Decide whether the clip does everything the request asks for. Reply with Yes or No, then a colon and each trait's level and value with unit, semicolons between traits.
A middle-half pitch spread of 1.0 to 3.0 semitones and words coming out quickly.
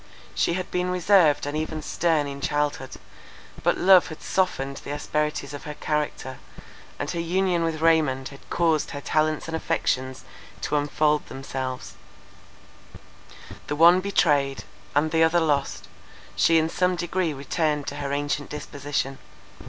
No: average, 2.7 semitones; average, 145 wpm